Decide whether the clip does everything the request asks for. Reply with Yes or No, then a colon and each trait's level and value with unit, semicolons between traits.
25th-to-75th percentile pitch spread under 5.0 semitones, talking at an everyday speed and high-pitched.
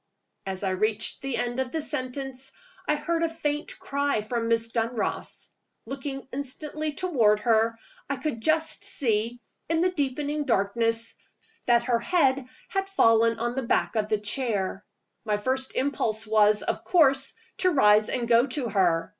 Yes: average, 4.4 semitones; average, 165 wpm; very high, 250 Hz